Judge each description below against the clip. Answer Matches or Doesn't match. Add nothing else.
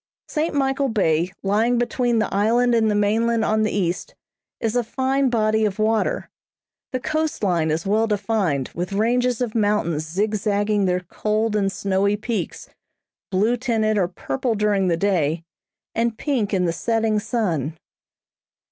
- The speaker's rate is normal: Matches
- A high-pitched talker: Matches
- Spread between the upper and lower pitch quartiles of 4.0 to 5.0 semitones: Doesn't match